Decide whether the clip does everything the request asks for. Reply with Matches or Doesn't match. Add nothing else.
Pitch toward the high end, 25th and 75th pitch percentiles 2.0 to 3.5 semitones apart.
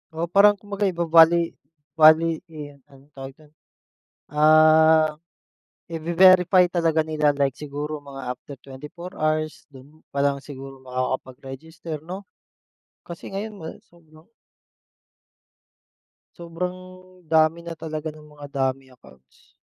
Doesn't match